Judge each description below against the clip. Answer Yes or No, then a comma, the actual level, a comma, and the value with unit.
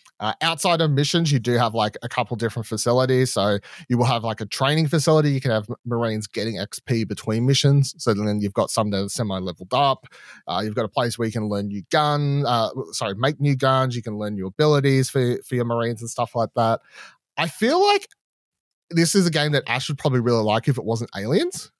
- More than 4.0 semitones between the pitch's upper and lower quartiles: Yes, average, 4.5 semitones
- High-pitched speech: No, low, 120 Hz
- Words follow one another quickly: Yes, fast, 230 wpm